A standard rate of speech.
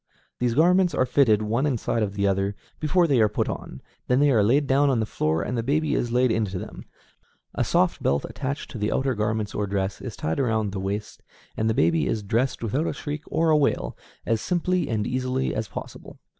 No: fast, 225 wpm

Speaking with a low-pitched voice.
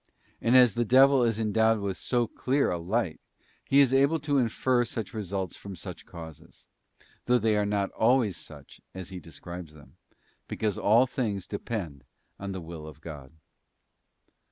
Yes: low, 105 Hz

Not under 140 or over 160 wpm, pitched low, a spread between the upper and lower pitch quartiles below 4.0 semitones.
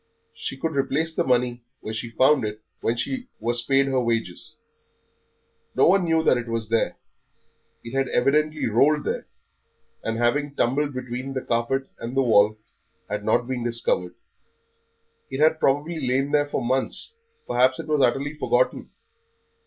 Yes: average, 155 wpm; low, 130 Hz; average, 3.6 semitones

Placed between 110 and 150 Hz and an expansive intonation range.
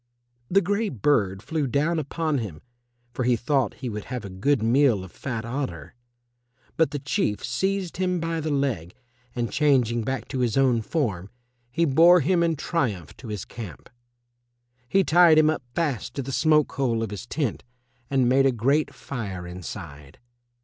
Yes: low, 135 Hz; wide, 5.9 semitones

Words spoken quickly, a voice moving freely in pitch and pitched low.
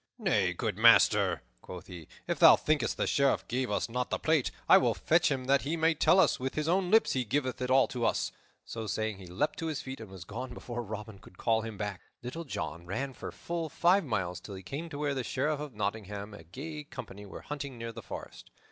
Yes: fast, 240 wpm; wide, 6.2 semitones; low, 125 Hz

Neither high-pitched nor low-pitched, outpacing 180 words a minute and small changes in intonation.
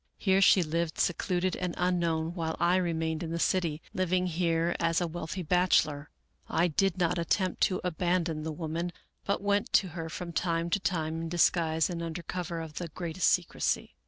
Yes: medium, 170 Hz; average, 190 wpm; narrow, 1.9 semitones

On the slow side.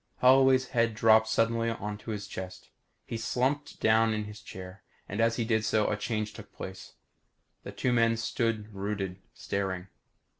No: average, 160 wpm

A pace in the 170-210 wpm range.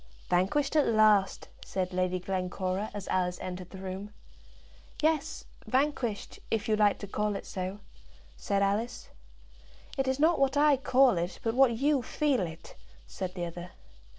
No: average, 155 wpm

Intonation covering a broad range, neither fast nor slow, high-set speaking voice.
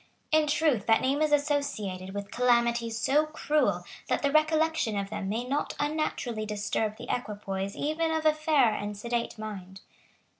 Yes: wide, 6.4 semitones; average, 160 wpm; high, 240 Hz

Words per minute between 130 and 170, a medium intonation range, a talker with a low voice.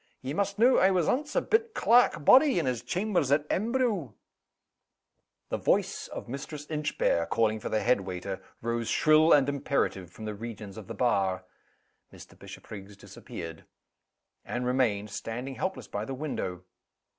No: average, 160 wpm; wide, 8.5 semitones; low, 130 Hz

